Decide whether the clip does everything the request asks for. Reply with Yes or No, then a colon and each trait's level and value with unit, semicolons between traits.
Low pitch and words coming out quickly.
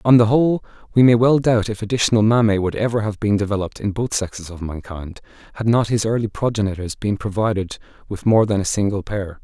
Yes: low, 105 Hz; fast, 210 wpm